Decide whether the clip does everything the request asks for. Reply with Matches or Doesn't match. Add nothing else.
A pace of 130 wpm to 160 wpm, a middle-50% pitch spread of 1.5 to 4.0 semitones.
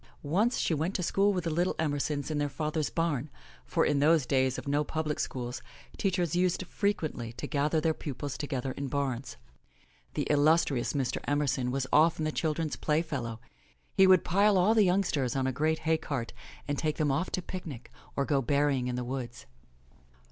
Doesn't match